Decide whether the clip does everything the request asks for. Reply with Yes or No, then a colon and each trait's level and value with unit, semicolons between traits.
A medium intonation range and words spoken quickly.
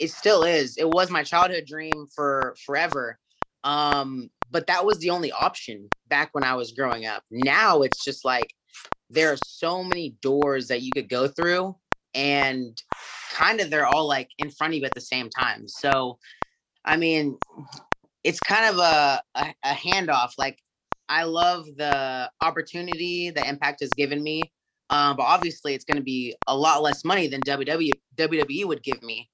No: average, 3.4 semitones; average, 180 wpm